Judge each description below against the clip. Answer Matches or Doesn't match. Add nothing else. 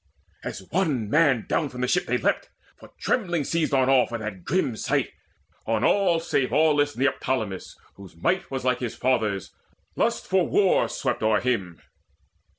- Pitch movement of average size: Doesn't match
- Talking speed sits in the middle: Matches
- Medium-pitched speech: Doesn't match